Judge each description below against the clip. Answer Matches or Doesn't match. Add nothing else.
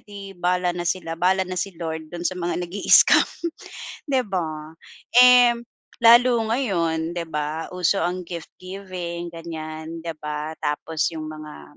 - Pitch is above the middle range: Doesn't match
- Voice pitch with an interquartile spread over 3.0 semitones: Doesn't match